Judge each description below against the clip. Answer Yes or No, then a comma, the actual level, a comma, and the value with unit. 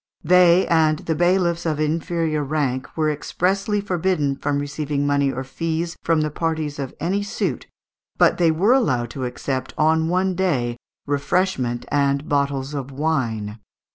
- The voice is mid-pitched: Yes, medium, 155 Hz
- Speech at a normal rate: Yes, average, 150 wpm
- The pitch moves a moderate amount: Yes, average, 3.6 semitones